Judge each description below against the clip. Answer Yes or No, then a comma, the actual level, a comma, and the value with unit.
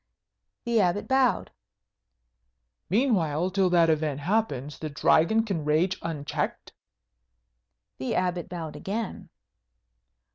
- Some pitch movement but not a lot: Yes, average, 4.8 semitones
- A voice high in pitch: No, medium, 175 Hz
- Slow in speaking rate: Yes, slow, 100 wpm